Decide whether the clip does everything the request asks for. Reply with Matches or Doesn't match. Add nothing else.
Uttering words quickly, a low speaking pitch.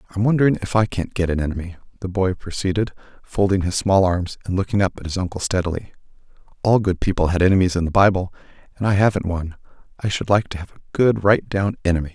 Matches